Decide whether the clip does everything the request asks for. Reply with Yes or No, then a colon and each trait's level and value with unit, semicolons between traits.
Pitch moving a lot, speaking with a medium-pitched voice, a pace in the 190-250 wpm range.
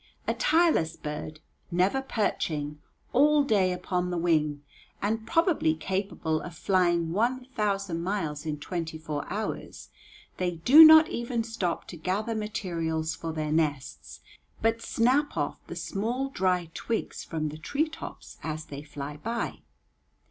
No: wide, 6.3 semitones; medium, 180 Hz; average, 140 wpm